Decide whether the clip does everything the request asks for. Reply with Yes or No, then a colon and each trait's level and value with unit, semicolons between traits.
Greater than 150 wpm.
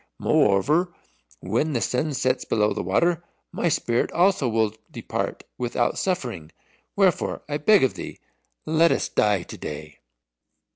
No: average, 140 wpm